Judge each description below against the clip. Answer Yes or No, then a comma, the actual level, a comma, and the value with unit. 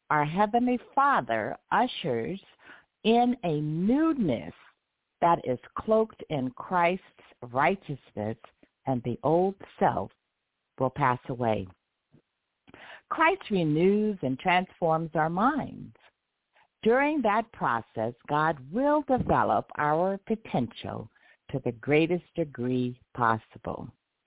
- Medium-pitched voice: Yes, medium, 165 Hz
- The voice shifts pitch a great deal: Yes, wide, 8.8 semitones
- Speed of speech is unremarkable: No, slow, 95 wpm